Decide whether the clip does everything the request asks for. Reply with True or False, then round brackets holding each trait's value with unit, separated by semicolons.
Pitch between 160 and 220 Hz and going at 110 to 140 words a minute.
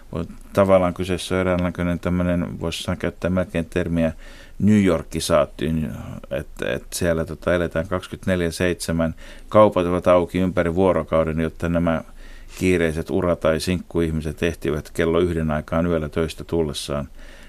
False (85 Hz; 125 wpm)